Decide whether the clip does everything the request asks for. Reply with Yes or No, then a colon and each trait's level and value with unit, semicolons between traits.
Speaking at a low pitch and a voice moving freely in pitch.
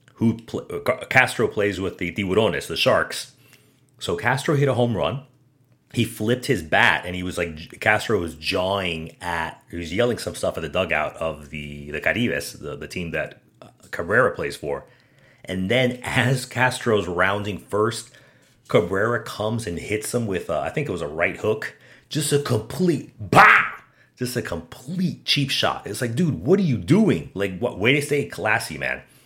Yes: low, 120 Hz; wide, 6.2 semitones